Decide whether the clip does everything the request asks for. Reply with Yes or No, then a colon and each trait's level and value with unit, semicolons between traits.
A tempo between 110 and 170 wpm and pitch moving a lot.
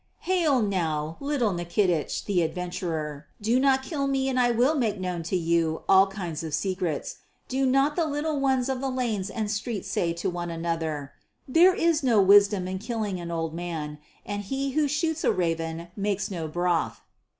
No: average, 185 wpm; wide, 7.6 semitones